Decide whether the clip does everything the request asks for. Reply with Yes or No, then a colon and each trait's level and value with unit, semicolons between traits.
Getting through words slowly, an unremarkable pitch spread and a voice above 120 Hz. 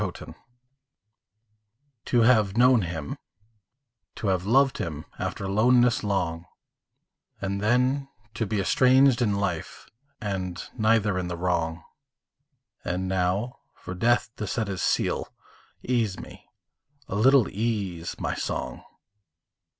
No: slow, 120 wpm; average, 4.6 semitones; low, 100 Hz